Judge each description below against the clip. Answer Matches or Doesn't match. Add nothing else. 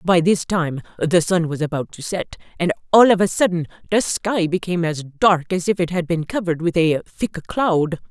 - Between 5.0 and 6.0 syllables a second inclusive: Matches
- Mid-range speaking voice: Matches